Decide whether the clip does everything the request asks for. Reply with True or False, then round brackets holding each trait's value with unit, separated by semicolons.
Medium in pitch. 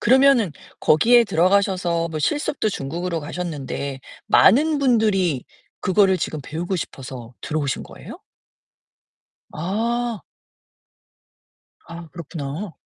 True (180 Hz)